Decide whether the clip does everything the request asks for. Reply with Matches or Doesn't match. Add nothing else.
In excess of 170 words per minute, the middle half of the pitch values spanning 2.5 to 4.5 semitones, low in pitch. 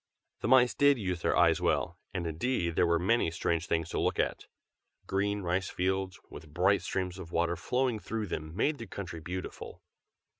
Matches